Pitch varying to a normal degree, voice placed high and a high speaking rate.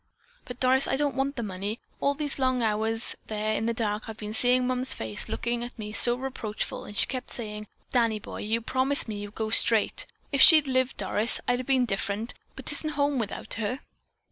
Yes: average, 3.4 semitones; high, 235 Hz; fast, 215 wpm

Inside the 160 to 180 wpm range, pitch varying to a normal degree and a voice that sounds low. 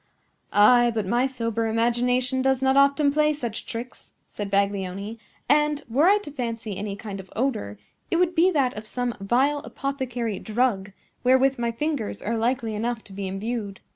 No: average, 170 wpm; average, 4.0 semitones; high, 240 Hz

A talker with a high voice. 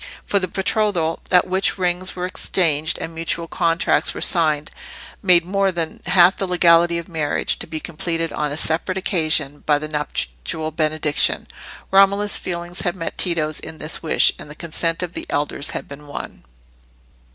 No: medium, 165 Hz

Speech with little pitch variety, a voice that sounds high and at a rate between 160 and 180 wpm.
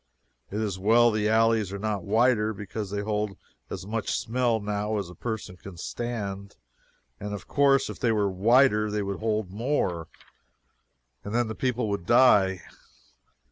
No: narrow, 2.3 semitones; low, 105 Hz; average, 165 wpm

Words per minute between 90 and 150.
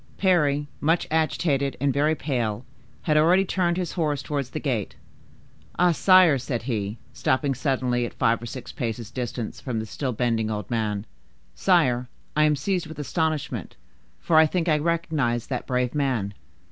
No: average, 165 wpm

